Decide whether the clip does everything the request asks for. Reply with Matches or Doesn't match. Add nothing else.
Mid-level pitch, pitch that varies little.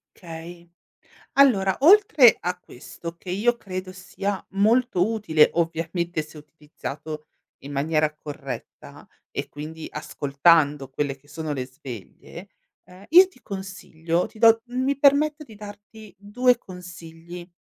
Doesn't match